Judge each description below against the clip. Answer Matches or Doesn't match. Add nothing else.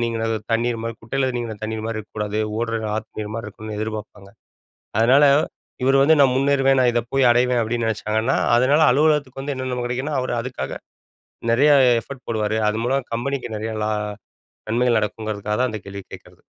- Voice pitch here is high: Doesn't match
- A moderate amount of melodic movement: Matches